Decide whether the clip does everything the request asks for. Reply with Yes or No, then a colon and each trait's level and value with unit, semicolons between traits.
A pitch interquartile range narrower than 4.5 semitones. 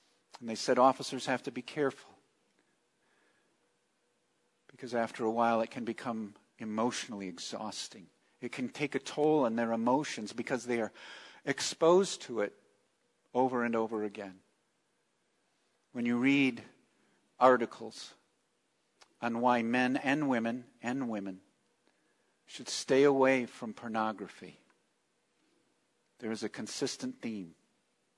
Yes: average, 2.8 semitones